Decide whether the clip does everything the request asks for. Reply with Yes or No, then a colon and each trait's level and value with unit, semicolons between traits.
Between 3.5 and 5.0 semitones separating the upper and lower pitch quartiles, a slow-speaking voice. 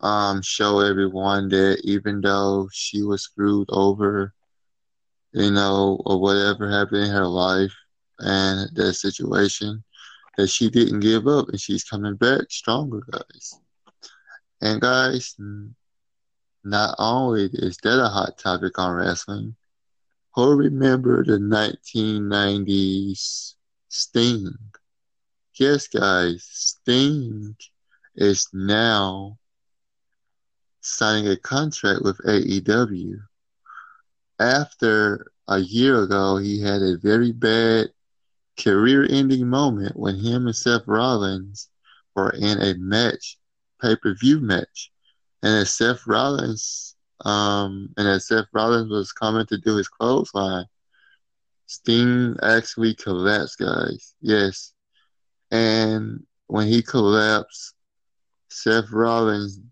No: narrow, 2.6 semitones; slow, 110 wpm